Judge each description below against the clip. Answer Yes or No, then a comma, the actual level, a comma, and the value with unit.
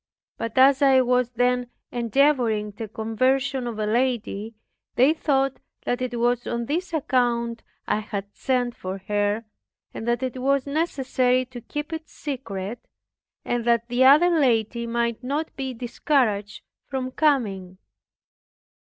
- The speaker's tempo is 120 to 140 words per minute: Yes, slow, 135 wpm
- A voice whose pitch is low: No, high, 245 Hz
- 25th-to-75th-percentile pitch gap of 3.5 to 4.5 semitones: No, average, 2.8 semitones